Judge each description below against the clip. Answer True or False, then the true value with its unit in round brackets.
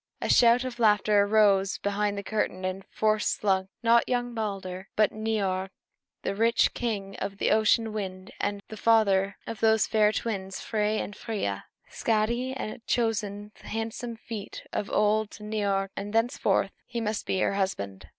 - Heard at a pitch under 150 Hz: False (210 Hz)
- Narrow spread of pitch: True (2.2 semitones)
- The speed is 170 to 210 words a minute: False (160 wpm)